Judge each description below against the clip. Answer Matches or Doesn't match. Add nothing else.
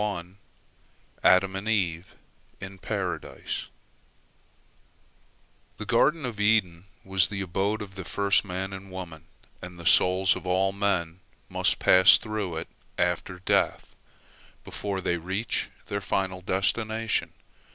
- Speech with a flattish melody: Matches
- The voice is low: Matches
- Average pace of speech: Doesn't match